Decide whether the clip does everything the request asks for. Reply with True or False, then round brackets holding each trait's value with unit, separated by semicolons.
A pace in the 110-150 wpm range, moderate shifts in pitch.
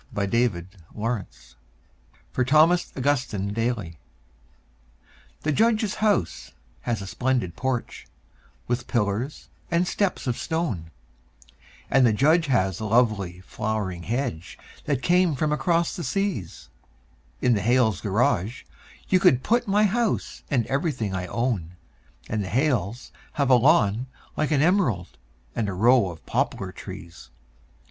False (140 wpm; 7.2 semitones)